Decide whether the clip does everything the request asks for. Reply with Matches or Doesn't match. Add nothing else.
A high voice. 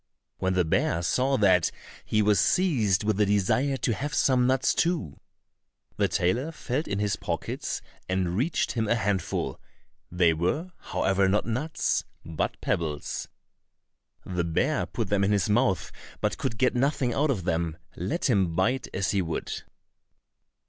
Doesn't match